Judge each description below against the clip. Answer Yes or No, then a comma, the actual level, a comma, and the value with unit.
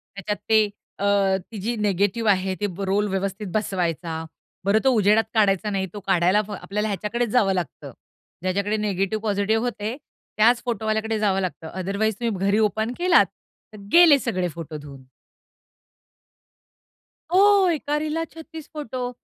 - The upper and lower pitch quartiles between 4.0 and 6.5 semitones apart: No, average, 3.2 semitones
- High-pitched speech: Yes, high, 210 Hz